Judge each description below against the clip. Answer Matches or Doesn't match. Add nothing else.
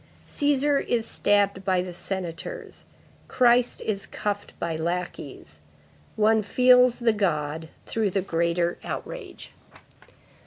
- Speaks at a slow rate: Matches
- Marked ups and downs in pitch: Matches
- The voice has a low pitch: Doesn't match